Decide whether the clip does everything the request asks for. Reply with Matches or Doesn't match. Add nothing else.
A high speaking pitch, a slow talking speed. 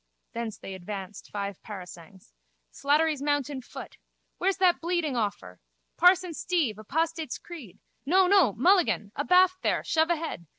Matches